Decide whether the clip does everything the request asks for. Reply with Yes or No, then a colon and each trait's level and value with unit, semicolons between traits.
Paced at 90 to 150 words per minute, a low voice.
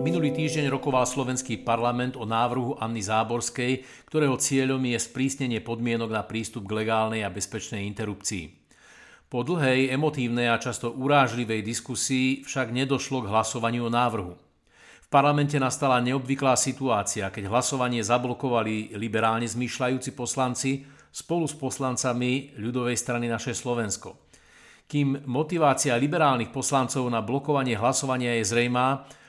Yes: average, 125 wpm; low, 125 Hz